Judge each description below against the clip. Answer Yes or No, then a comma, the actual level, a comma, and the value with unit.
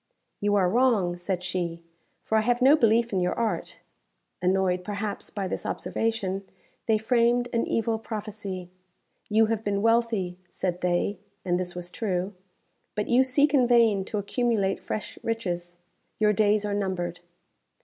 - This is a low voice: No, high, 205 Hz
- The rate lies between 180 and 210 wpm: No, average, 155 wpm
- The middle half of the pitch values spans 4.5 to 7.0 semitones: No, average, 3.8 semitones